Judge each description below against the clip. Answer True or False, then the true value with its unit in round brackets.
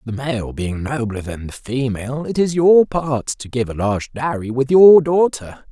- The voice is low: True (130 Hz)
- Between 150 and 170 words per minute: False (200 wpm)